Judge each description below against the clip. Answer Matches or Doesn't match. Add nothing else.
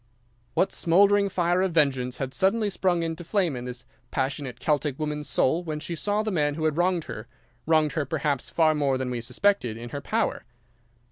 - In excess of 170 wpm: Matches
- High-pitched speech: Doesn't match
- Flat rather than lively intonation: Doesn't match